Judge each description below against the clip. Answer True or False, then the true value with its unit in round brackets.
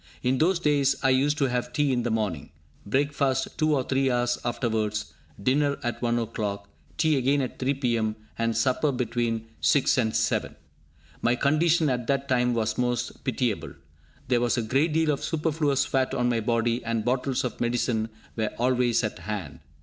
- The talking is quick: False (180 wpm)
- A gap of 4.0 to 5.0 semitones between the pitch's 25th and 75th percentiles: False (3.2 semitones)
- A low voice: True (125 Hz)